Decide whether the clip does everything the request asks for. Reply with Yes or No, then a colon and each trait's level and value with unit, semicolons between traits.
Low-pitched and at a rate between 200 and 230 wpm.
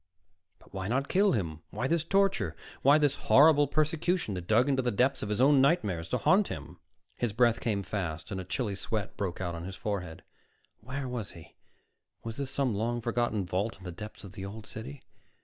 Yes: low, 110 Hz; fast, 205 wpm